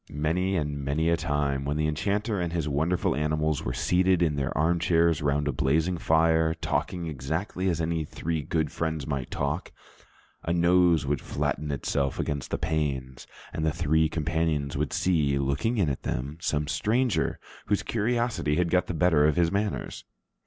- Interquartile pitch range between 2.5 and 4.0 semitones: Yes, average, 3.0 semitones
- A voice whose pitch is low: Yes, very low, 80 Hz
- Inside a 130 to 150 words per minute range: No, average, 175 wpm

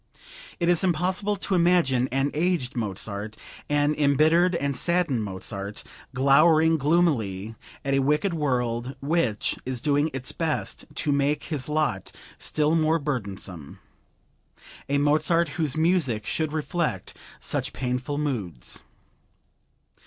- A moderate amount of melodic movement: Yes, average, 4.5 semitones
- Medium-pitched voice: Yes, medium, 145 Hz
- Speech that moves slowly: Yes, slow, 120 wpm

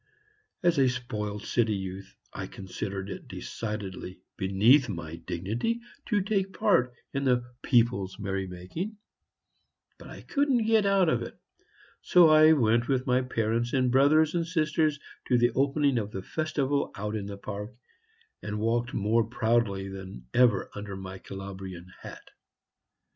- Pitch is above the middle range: No, low, 115 Hz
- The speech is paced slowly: No, average, 150 wpm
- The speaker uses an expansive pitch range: Yes, wide, 6.3 semitones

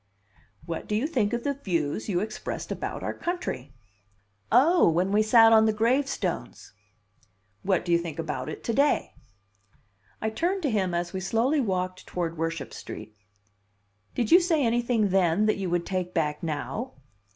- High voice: Yes, high, 205 Hz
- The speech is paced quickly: No, average, 170 wpm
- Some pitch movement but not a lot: No, wide, 5.8 semitones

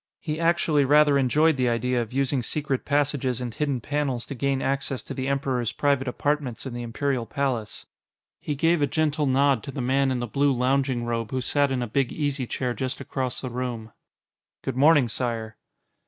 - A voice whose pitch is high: No, low, 135 Hz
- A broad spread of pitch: No, narrow, 2.6 semitones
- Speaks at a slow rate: No, average, 195 wpm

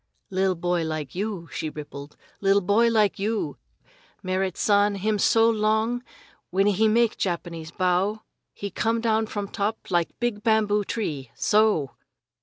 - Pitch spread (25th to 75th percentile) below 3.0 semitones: No, average, 3.5 semitones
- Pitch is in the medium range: No, high, 205 Hz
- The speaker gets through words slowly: No, average, 145 wpm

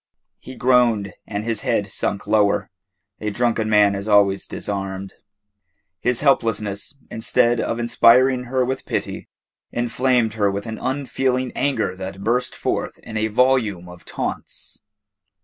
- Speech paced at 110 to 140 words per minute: Yes, slow, 135 wpm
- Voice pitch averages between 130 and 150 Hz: No, low, 110 Hz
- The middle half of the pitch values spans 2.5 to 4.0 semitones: Yes, average, 3.6 semitones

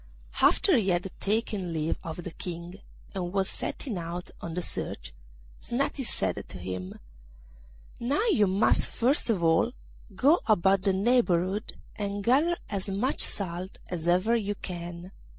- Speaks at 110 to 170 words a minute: Yes, average, 150 wpm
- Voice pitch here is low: No, high, 195 Hz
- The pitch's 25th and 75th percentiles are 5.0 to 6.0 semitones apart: No, average, 4.5 semitones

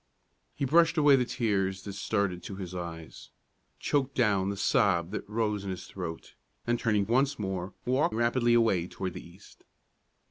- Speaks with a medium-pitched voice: No, low, 100 Hz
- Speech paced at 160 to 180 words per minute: Yes, average, 170 wpm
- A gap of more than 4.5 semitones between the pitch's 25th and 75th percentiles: No, average, 4.1 semitones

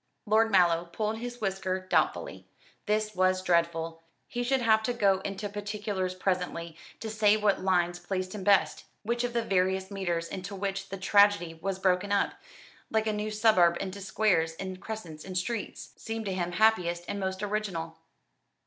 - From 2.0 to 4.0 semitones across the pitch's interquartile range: Yes, average, 2.8 semitones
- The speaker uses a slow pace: No, average, 170 wpm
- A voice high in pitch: Yes, high, 195 Hz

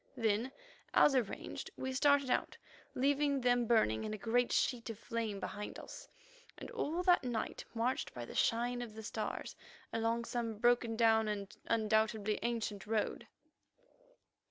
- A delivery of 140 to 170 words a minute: Yes, average, 150 wpm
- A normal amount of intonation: No, narrow, 2.3 semitones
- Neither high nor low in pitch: No, high, 230 Hz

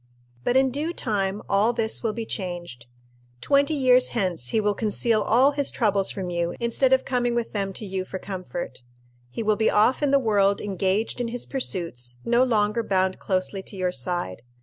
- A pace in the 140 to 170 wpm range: No, average, 195 wpm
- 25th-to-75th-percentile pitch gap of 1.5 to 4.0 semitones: No, average, 4.4 semitones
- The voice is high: Yes, high, 210 Hz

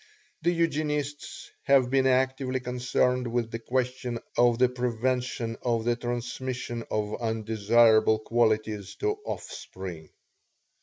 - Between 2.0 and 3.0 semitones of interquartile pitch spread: Yes, narrow, 2.4 semitones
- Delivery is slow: Yes, slow, 110 wpm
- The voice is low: Yes, low, 120 Hz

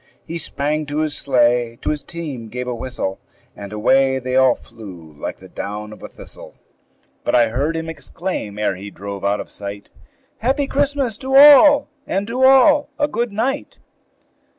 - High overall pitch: No, low, 135 Hz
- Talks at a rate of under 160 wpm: No, average, 175 wpm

